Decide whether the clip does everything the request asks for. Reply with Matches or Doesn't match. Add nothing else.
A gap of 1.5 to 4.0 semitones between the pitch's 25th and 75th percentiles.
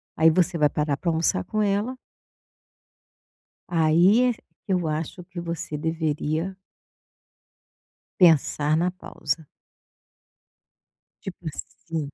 Matches